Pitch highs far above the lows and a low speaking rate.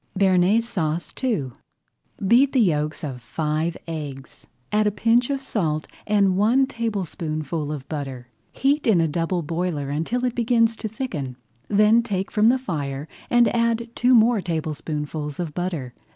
No: wide, 7.0 semitones; average, 150 wpm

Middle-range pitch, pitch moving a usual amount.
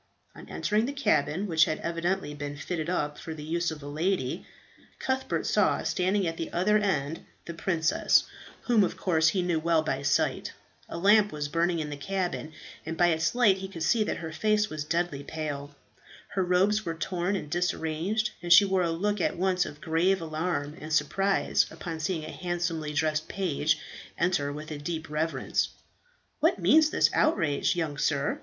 Yes: medium, 170 Hz; average, 3.6 semitones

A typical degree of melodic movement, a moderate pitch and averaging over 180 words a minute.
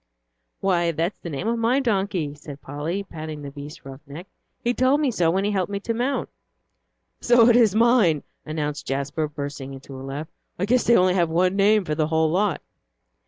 No: wide, 6.1 semitones; medium, 170 Hz; fast, 205 wpm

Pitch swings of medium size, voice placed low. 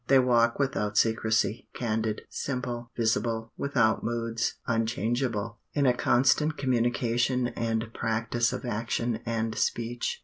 No: narrow, 1.5 semitones; low, 115 Hz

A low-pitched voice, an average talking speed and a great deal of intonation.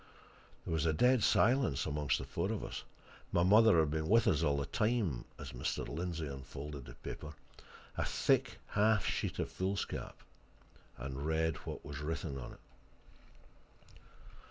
Yes: very low, 80 Hz; average, 155 wpm; wide, 7.0 semitones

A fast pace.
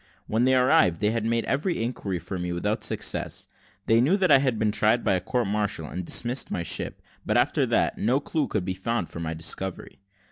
Yes: fast, 220 wpm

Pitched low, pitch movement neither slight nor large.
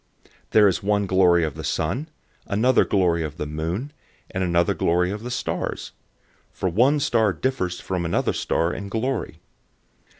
Yes: very low, 95 Hz; average, 4.7 semitones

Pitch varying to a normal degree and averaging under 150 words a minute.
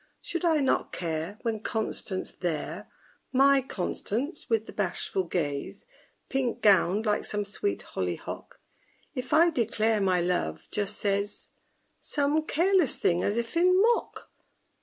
No: wide, 6.8 semitones; average, 140 wpm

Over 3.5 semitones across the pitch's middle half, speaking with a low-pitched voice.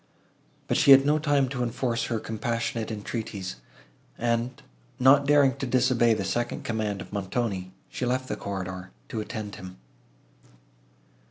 Yes: average, 3.9 semitones; low, 115 Hz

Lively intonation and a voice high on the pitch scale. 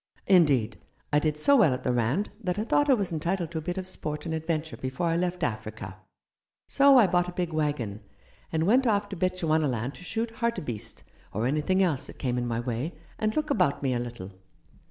No: wide, 6.7 semitones; medium, 160 Hz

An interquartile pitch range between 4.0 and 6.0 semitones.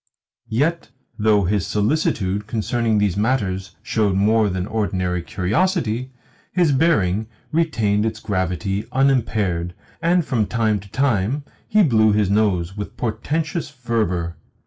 Yes: average, 4.9 semitones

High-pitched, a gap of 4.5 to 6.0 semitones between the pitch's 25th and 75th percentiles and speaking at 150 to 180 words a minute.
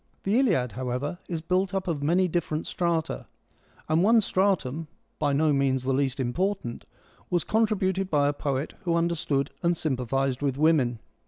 No: medium, 155 Hz; average, 5.1 semitones; average, 175 wpm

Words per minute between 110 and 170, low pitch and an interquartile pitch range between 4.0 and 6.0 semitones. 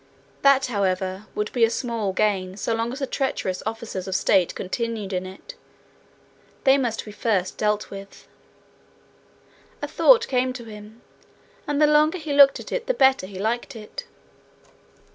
No: average, 160 wpm; high, 225 Hz; average, 5.3 semitones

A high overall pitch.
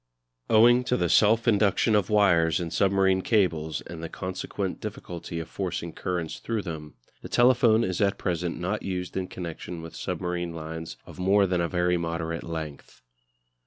No: very low, 90 Hz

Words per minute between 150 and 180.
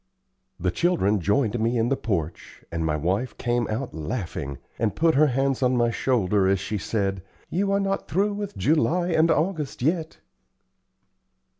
Yes: average, 165 wpm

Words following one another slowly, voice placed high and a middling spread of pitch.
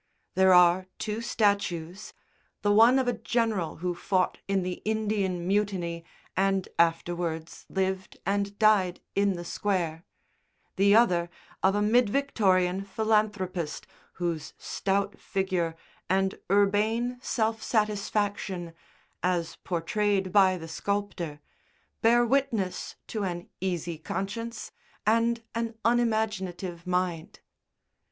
Yes: slow, 110 wpm; high, 195 Hz; average, 3.2 semitones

